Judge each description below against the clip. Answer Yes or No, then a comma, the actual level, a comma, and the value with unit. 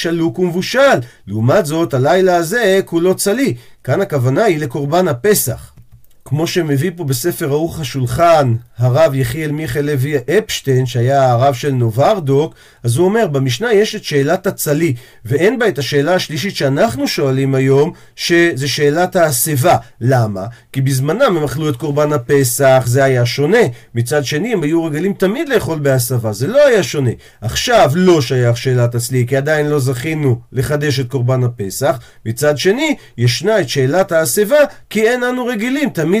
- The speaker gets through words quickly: Yes, fast, 155 wpm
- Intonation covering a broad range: No, average, 4.6 semitones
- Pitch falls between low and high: Yes, medium, 145 Hz